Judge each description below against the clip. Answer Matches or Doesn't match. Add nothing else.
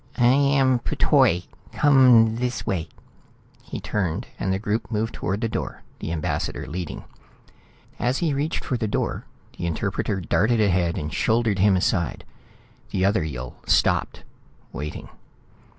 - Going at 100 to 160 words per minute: Matches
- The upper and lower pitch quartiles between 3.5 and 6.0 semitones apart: Matches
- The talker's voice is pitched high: Doesn't match